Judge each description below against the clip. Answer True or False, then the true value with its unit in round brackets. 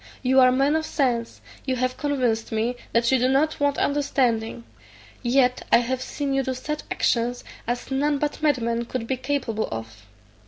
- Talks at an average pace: True (180 wpm)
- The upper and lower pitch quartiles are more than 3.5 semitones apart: False (2.9 semitones)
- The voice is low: False (255 Hz)